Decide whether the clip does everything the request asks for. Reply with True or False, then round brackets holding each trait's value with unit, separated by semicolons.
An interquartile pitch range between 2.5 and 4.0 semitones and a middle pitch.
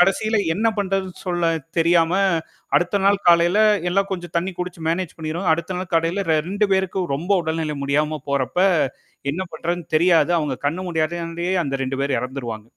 True (3.0 semitones; 170 Hz)